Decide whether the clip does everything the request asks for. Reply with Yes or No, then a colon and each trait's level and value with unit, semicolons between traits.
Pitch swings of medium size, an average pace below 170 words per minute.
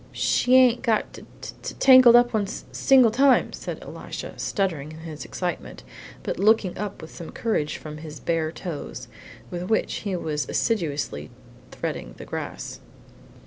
No: wide, 6.5 semitones; average, 155 wpm